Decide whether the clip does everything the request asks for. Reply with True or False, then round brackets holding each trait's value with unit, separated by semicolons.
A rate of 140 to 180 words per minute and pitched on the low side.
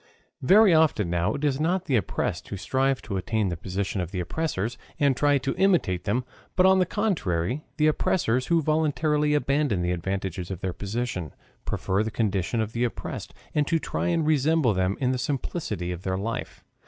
False (190 wpm; 125 Hz)